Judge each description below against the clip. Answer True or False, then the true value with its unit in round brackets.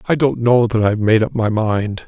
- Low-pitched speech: True (115 Hz)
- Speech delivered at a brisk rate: True (260 wpm)